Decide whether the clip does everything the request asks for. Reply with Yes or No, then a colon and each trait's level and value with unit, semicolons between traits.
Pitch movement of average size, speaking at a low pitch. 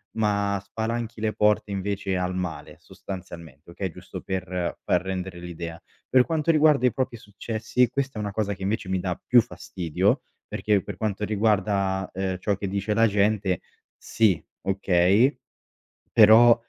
Yes: average, 3.0 semitones; low, 100 Hz